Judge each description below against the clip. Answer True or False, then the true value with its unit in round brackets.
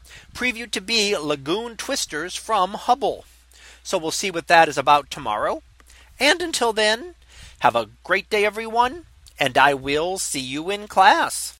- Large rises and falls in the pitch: True (7.9 semitones)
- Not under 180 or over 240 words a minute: False (155 wpm)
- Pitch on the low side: False (200 Hz)